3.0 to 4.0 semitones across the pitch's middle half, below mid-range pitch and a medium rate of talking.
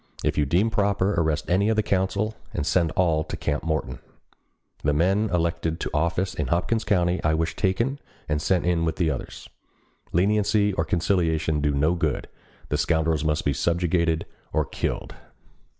Yes: average, 3.5 semitones; very low, 85 Hz; average, 165 wpm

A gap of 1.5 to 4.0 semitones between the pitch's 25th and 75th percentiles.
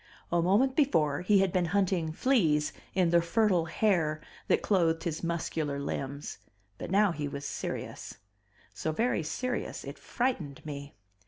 No: average, 4.7 semitones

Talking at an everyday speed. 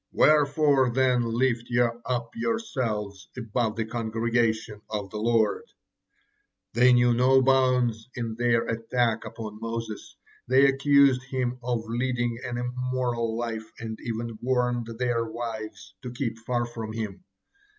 No: slow, 130 wpm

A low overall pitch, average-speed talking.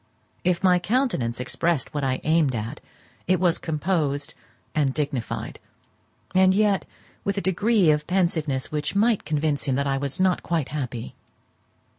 No: medium, 155 Hz; average, 150 wpm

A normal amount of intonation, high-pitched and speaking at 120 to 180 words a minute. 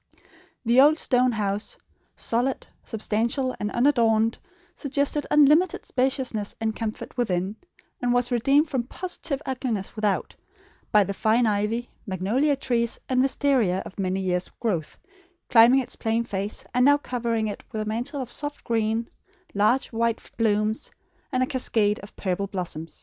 Yes: average, 3.7 semitones; high, 230 Hz; average, 145 wpm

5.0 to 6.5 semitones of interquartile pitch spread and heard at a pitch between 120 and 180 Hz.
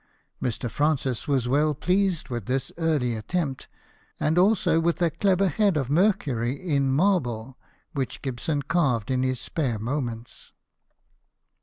Yes: average, 5.3 semitones; medium, 140 Hz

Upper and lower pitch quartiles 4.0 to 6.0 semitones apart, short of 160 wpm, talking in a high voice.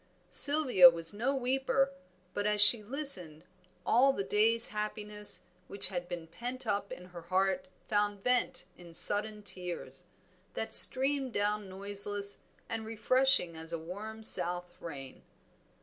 Yes: average, 5.1 semitones; slow, 135 wpm; high, 205 Hz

